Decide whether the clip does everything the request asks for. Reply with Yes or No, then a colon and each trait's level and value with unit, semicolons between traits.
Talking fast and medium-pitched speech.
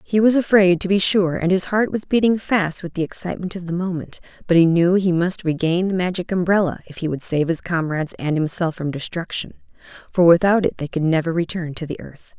Yes: fast, 230 wpm; medium, 175 Hz